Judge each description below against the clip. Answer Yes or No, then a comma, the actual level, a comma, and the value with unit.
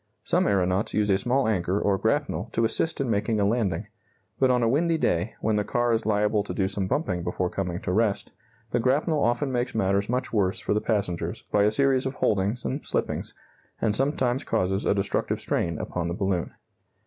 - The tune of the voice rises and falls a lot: No, average, 4.1 semitones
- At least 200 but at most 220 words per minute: Yes, fast, 205 wpm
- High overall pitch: No, low, 105 Hz